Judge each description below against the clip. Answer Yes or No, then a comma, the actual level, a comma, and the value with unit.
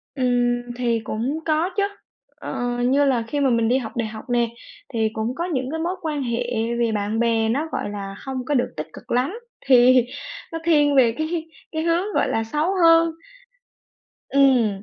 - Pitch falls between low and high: No, very high, 255 Hz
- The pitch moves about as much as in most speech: Yes, average, 4.8 semitones